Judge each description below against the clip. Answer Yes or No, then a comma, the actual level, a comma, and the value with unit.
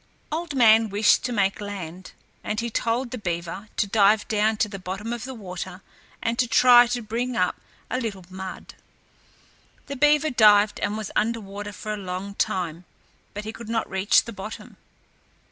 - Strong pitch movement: No, average, 3.1 semitones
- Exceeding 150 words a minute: Yes, average, 180 wpm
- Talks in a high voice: Yes, high, 215 Hz